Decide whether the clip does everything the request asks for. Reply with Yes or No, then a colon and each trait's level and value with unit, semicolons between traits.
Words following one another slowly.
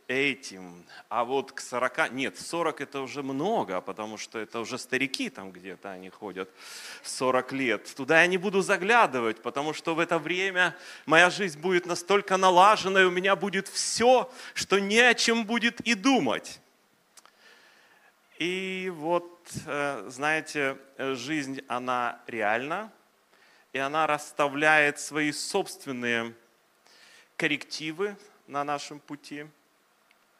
No: average, 125 wpm